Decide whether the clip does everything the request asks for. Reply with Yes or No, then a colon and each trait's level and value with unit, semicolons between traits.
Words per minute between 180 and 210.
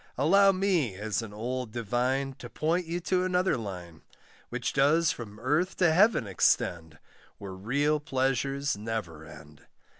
No: average, 145 wpm